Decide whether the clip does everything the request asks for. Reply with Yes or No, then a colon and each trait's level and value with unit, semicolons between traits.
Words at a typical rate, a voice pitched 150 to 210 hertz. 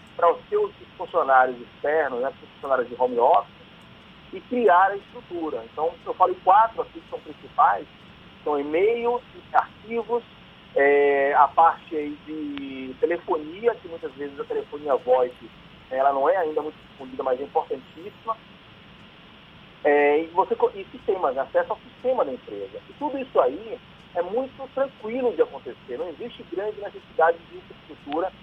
Yes: average, 150 wpm; high, 190 Hz